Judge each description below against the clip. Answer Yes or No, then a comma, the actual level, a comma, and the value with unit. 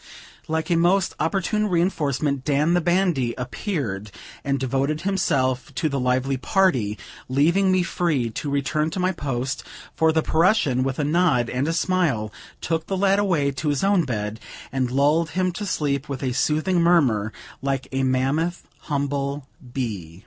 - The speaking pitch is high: No, medium, 145 Hz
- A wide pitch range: No, average, 4.8 semitones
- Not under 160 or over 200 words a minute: Yes, average, 165 wpm